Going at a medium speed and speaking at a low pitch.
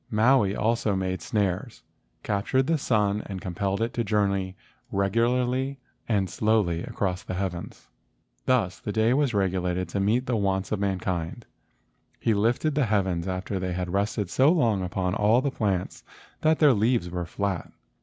Yes: average, 165 wpm; low, 100 Hz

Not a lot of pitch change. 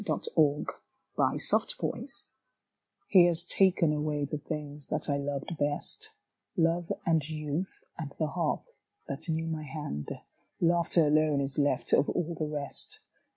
Yes: narrow, 2.3 semitones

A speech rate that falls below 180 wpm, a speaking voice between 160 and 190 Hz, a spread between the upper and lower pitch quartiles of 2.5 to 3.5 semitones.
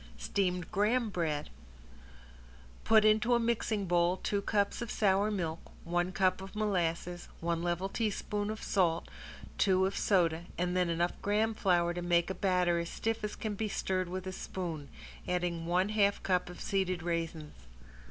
Yes: average, 165 wpm; medium, 185 Hz; average, 3.0 semitones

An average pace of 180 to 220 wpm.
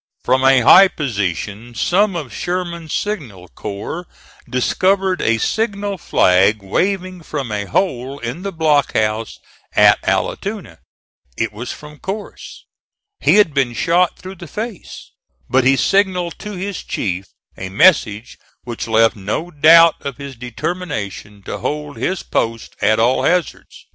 No: average, 140 wpm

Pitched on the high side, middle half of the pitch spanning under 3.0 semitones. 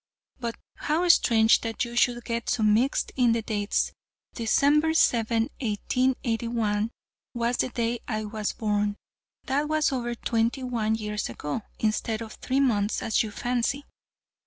Yes: high, 230 Hz; narrow, 2.4 semitones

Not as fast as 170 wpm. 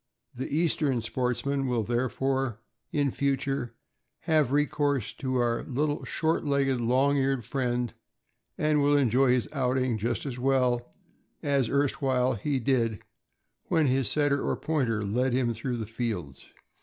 Yes: average, 140 wpm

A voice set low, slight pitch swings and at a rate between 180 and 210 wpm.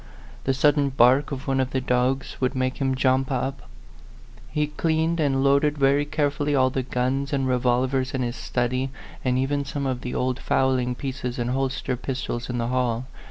Yes: low, 130 Hz; narrow, 1.7 semitones; average, 190 wpm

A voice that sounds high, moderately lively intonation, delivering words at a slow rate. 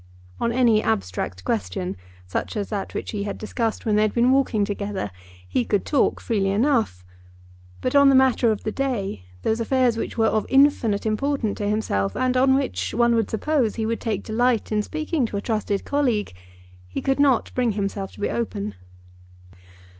No: high, 220 Hz; average, 3.9 semitones; average, 185 wpm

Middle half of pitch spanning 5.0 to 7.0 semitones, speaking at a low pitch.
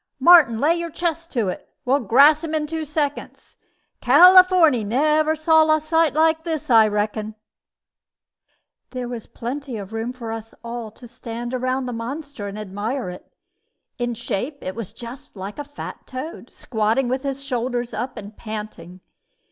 No: average, 5.3 semitones; very high, 255 Hz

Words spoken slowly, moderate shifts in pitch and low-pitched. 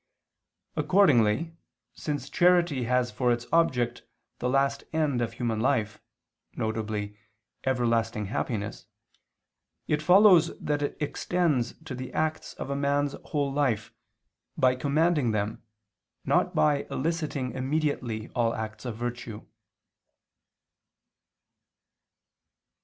Yes: slow, 105 wpm; average, 4.4 semitones; low, 130 Hz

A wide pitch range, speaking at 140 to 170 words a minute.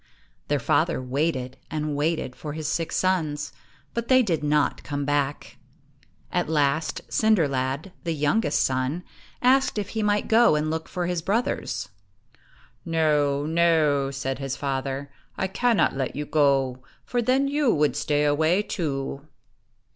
No: average, 4.3 semitones; average, 145 wpm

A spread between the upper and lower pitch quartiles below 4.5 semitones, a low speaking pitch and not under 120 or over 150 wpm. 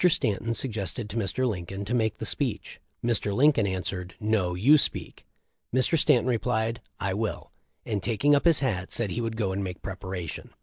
No: average, 4.1 semitones; low, 110 Hz; average, 185 wpm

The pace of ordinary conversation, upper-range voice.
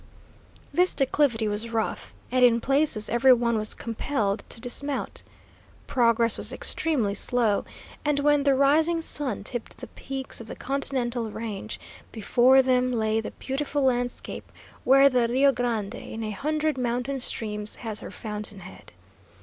Yes: average, 150 wpm; high, 245 Hz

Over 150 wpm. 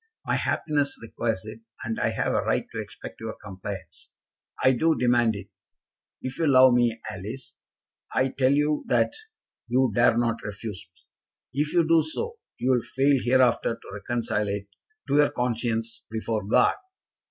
Yes: average, 165 wpm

